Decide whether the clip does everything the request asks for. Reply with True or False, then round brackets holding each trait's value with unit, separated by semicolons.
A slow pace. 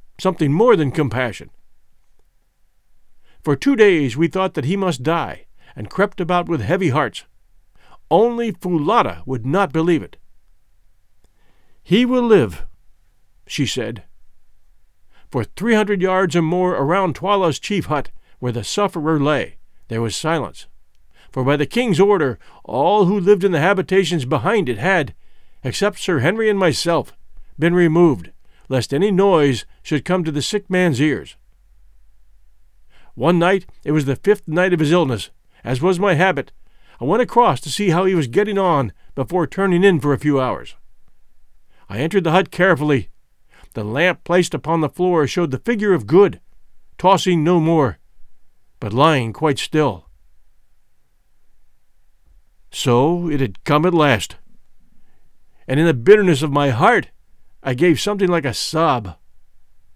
False (150 wpm)